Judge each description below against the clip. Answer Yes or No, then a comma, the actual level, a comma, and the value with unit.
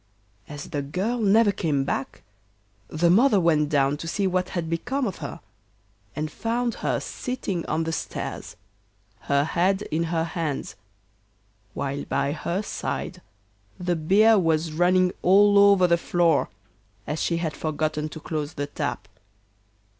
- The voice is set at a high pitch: No, medium, 170 Hz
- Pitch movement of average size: Yes, average, 4.0 semitones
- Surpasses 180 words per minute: No, average, 145 wpm